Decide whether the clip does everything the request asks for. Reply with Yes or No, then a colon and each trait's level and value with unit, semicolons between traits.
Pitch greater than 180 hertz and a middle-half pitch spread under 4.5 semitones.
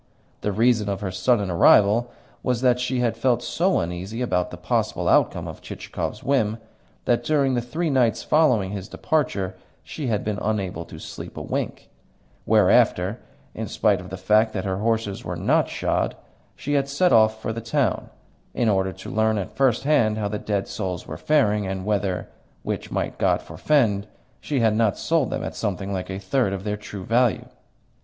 No: low, 110 Hz; average, 4.1 semitones